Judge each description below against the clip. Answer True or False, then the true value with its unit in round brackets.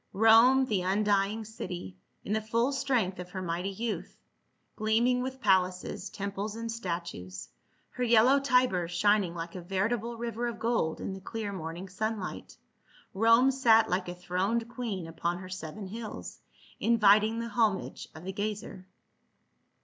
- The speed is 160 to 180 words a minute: False (150 wpm)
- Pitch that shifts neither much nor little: True (3.9 semitones)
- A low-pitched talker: False (210 Hz)